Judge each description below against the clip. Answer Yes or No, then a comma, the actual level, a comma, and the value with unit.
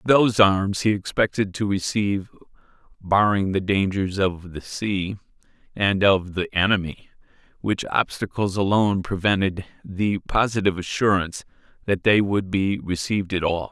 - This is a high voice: No, low, 100 Hz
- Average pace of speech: No, slow, 130 wpm